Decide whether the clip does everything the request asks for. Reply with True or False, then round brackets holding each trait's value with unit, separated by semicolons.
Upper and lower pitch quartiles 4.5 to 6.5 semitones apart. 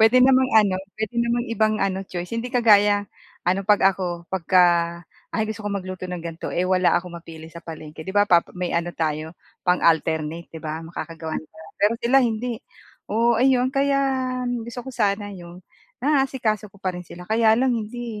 True (5.0 semitones)